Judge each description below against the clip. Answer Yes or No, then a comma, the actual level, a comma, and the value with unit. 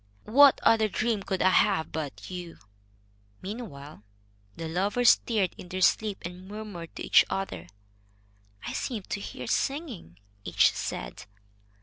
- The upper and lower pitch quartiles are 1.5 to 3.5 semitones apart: No, average, 4.6 semitones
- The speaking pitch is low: No, high, 190 Hz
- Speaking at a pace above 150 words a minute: No, slow, 135 wpm